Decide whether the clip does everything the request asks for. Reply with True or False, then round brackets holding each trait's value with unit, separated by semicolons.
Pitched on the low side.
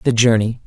True (115 Hz)